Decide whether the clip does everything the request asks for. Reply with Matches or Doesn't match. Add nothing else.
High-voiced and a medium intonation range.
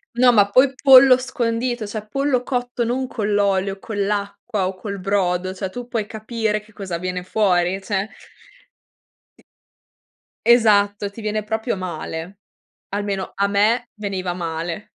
Matches